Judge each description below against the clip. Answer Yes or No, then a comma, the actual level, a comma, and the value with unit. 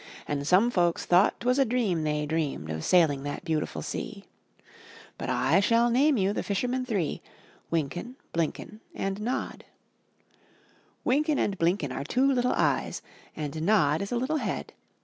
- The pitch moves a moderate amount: No, wide, 7.7 semitones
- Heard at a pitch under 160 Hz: No, high, 190 Hz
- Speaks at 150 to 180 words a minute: Yes, average, 160 wpm